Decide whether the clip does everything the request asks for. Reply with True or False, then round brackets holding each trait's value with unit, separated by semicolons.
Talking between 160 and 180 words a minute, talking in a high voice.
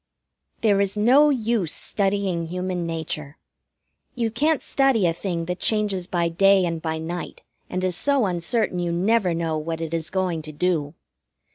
False (165 wpm; 180 Hz)